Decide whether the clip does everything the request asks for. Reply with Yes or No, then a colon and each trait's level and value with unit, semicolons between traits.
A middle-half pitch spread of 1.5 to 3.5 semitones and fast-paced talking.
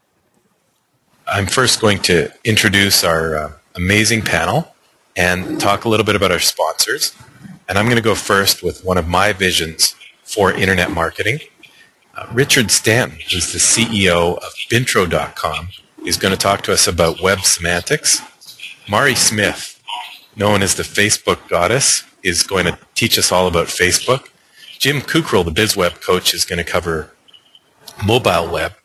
No: average, 2.8 semitones; average, 155 wpm